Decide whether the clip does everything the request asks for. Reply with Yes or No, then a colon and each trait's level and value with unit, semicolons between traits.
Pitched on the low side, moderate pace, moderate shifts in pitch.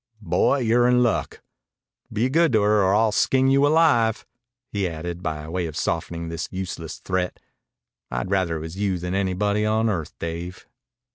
Yes: very low, 95 Hz; average, 170 wpm; average, 4.8 semitones